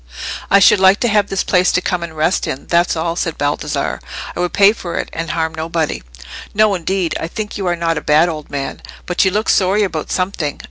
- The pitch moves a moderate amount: Yes, average, 3.1 semitones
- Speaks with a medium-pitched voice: Yes, medium, 175 Hz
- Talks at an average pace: No, fast, 230 wpm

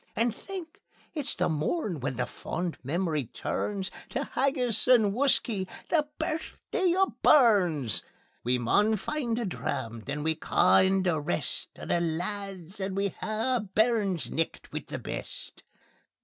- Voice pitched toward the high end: Yes, high, 200 Hz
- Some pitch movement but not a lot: No, wide, 6.9 semitones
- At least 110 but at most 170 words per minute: Yes, average, 150 wpm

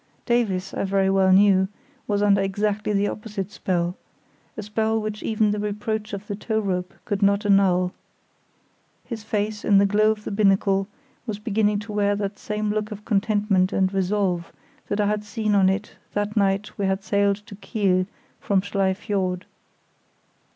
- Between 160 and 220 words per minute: Yes, average, 170 wpm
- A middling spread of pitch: No, narrow, 1.5 semitones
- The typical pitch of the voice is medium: No, high, 205 Hz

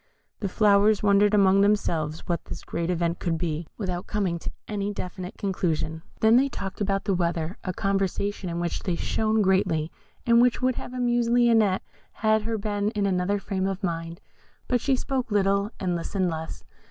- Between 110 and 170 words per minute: No, average, 180 wpm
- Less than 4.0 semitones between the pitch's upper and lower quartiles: Yes, average, 3.3 semitones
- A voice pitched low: No, high, 195 Hz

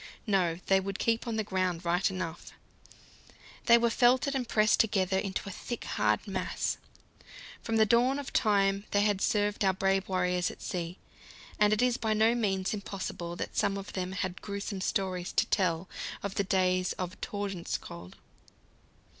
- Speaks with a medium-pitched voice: No, high, 195 Hz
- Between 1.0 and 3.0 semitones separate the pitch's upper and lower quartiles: Yes, narrow, 2.6 semitones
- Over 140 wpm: Yes, average, 170 wpm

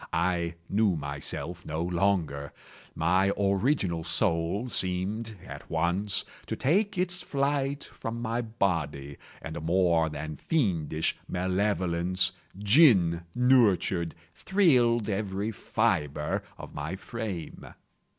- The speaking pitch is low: Yes, very low, 95 Hz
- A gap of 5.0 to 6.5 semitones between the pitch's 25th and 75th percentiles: Yes, wide, 5.4 semitones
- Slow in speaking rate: Yes, slow, 105 wpm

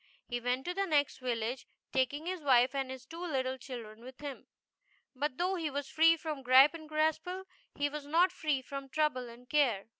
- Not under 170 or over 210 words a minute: Yes, average, 200 wpm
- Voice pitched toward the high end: Yes, very high, 280 Hz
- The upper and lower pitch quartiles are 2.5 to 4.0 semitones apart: Yes, average, 3.5 semitones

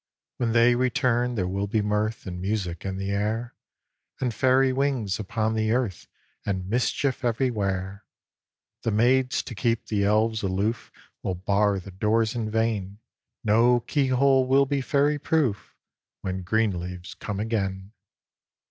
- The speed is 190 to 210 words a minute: No, average, 150 wpm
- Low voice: Yes, low, 110 Hz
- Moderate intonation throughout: Yes, average, 3.8 semitones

